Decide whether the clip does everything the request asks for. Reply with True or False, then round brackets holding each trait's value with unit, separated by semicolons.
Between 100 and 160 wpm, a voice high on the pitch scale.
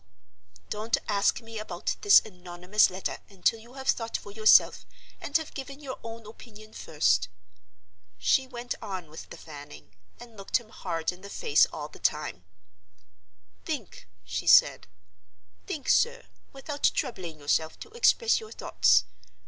True (150 wpm; 215 Hz)